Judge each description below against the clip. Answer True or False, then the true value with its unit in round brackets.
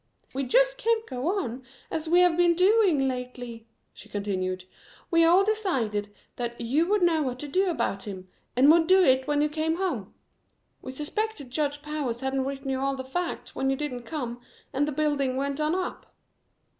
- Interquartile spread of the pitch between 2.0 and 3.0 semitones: False (5.4 semitones)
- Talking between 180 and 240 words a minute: True (190 wpm)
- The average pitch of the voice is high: True (285 Hz)